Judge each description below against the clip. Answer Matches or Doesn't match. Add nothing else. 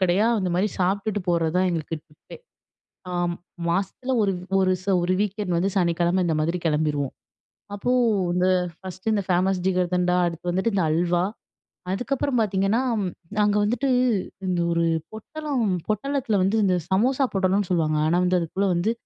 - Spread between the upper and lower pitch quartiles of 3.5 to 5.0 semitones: Doesn't match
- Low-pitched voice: Doesn't match